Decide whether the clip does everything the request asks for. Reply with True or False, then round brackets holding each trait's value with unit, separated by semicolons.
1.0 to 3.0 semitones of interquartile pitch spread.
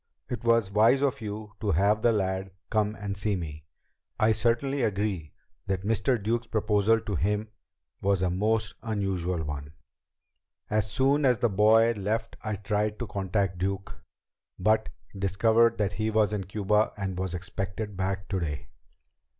True (2.4 semitones)